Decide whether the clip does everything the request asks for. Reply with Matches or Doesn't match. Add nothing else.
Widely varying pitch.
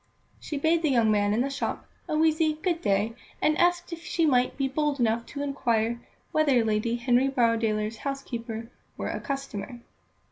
Doesn't match